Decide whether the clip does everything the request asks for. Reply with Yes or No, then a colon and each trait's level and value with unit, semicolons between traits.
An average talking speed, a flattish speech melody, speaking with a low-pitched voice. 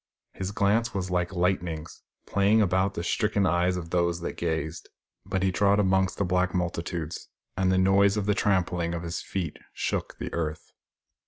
Yes: average, 175 wpm; narrow, 2.3 semitones; very low, 90 Hz